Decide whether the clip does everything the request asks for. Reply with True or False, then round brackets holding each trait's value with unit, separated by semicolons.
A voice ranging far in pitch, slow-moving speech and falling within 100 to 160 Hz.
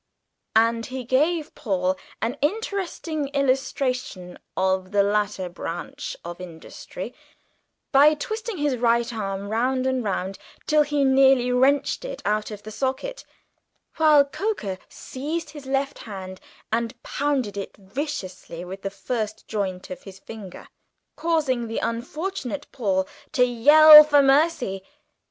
False (6.5 semitones; 130 wpm; 250 Hz)